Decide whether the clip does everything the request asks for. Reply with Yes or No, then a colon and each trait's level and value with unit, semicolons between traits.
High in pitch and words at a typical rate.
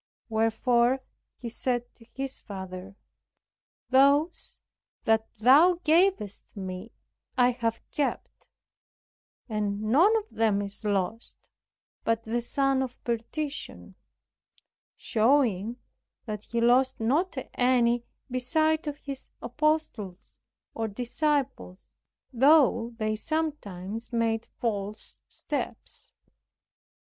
No: high, 235 Hz; slow, 95 wpm